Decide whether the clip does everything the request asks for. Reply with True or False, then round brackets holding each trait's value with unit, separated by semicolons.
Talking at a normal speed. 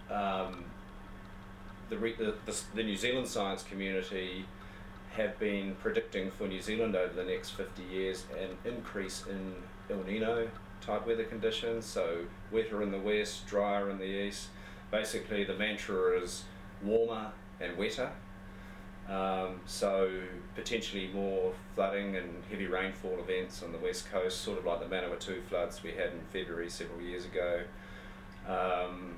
True (150 wpm)